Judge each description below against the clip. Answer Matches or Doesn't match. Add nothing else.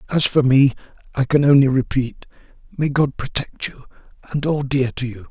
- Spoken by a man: Matches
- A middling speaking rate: Matches